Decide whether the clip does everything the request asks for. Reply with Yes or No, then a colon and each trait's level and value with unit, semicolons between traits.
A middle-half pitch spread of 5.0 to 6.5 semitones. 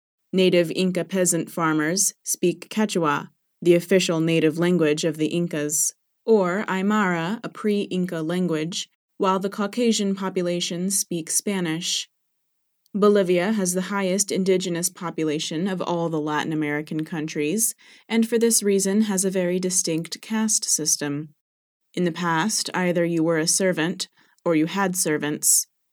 No: average, 3.1 semitones